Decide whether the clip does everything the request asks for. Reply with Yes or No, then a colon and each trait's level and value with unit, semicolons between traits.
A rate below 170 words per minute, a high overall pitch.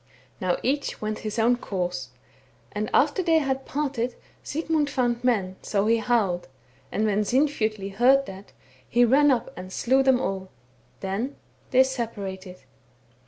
Yes: average, 155 wpm; high, 235 Hz